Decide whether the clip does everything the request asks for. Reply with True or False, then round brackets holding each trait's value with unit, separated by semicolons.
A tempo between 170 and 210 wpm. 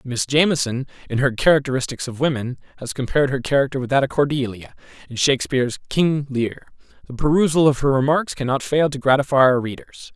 True (175 wpm)